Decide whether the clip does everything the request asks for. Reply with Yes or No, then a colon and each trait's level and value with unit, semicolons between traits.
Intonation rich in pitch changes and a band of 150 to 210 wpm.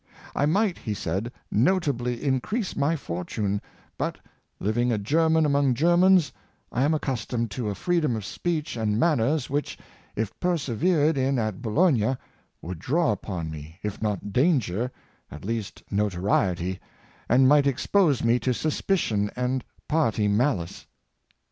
No: wide, 6.5 semitones; average, 140 wpm